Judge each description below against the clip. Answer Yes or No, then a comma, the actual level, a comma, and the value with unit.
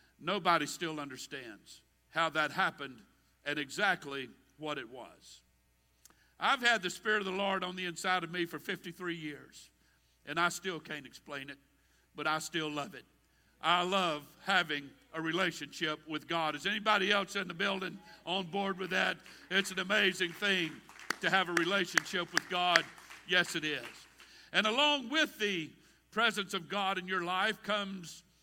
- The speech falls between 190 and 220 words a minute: No, average, 165 wpm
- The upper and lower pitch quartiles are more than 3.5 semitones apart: Yes, average, 4.1 semitones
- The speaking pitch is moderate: Yes, medium, 180 Hz